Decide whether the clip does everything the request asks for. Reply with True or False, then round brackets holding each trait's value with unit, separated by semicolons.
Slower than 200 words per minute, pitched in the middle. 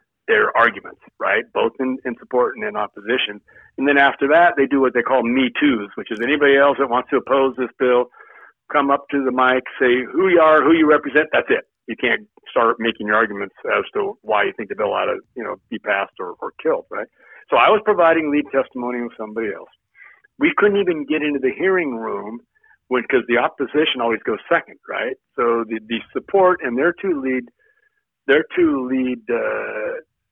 False (205 wpm; 150 Hz)